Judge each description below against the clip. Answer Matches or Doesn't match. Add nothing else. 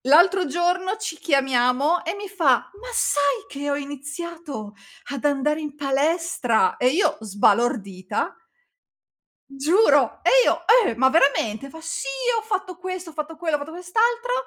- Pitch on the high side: Matches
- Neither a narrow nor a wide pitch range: Matches